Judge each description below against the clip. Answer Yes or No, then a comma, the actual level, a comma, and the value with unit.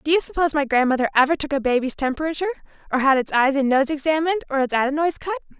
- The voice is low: No, very high, 290 Hz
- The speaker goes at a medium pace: No, fast, 225 wpm